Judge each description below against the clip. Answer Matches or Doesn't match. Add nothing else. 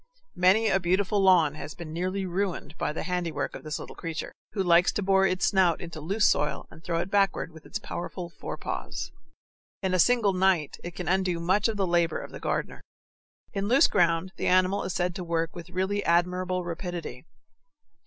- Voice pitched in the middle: Matches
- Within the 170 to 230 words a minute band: Matches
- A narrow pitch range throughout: Matches